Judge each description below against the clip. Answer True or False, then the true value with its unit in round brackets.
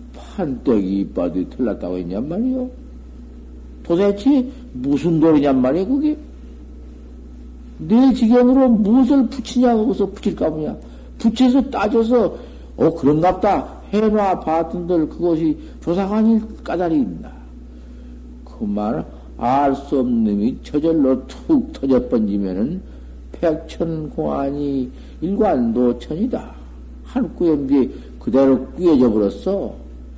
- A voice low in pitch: False (150 Hz)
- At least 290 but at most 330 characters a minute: False (235 characters per minute)